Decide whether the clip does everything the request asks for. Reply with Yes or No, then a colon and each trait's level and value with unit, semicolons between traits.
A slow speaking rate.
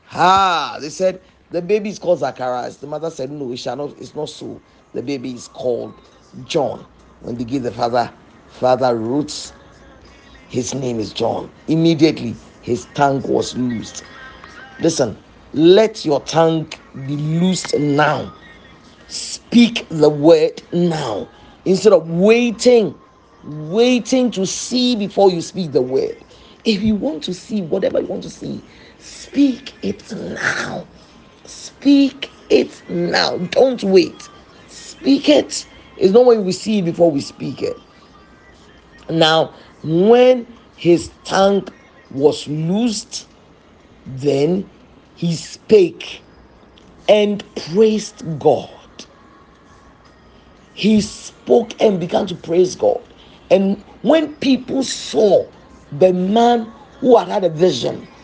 Yes: slow, 125 wpm